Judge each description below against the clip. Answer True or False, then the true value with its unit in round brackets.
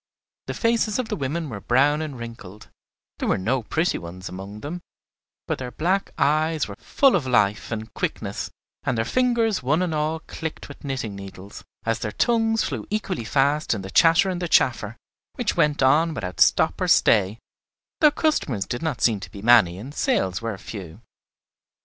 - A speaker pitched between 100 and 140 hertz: True (135 Hz)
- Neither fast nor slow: True (185 wpm)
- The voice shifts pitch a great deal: True (7.6 semitones)